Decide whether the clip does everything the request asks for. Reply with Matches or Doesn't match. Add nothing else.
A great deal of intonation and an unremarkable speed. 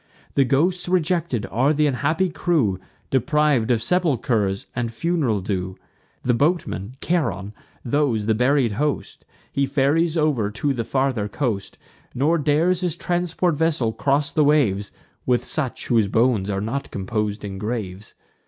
Matches